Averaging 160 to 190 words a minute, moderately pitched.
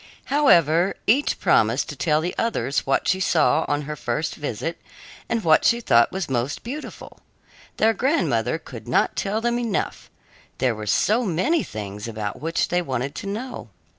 Yes: average, 165 wpm; medium, 170 Hz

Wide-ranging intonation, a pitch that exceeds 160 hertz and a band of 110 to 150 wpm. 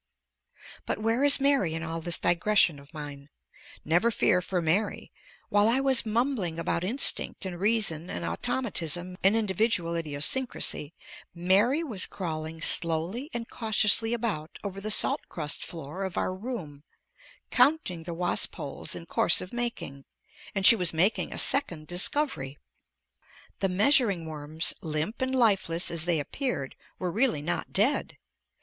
Yes: wide, 5.9 semitones; medium, 185 Hz; average, 145 wpm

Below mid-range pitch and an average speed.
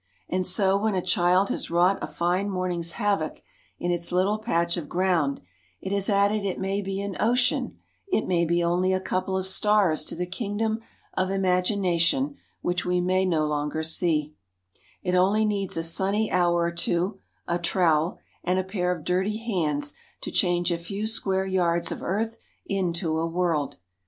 No: medium, 185 Hz; average, 180 wpm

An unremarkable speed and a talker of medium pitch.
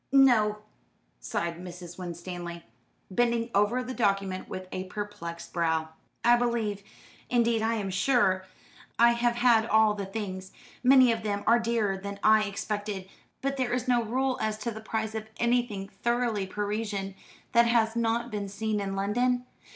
No: average, 160 wpm; high, 215 Hz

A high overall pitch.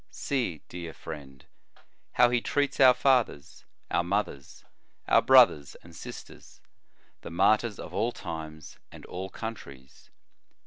No: very low, 90 Hz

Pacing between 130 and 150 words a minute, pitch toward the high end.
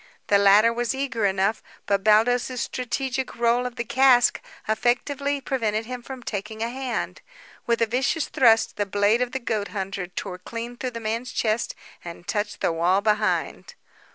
No: average, 170 wpm; high, 230 Hz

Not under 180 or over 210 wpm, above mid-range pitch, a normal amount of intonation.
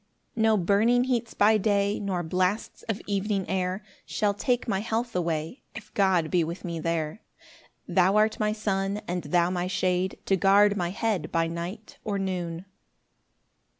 No: average, 165 wpm; high, 195 Hz; average, 3.1 semitones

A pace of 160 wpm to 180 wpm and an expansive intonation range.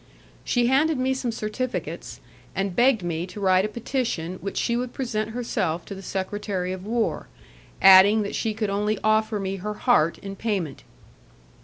No: average, 170 wpm; average, 3.7 semitones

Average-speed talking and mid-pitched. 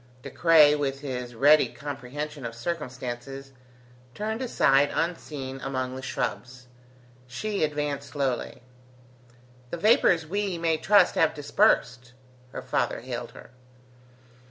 No: slow, 115 wpm; medium, 145 Hz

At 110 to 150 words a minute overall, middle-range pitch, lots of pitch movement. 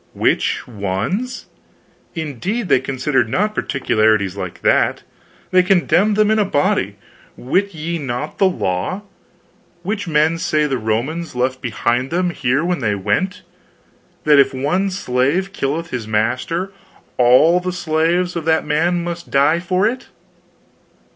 Yes: average, 140 wpm; medium, 155 Hz; wide, 6.3 semitones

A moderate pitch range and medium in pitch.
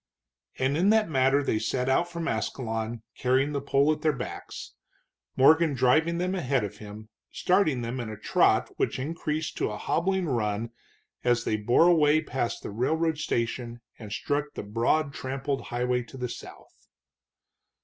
No: average, 4.9 semitones; low, 130 Hz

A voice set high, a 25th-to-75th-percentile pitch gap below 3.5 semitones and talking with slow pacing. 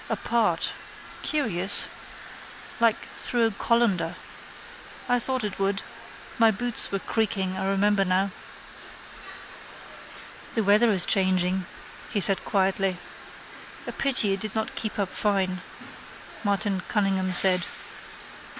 Yes: high, 200 Hz; average, 2.7 semitones; slow, 115 wpm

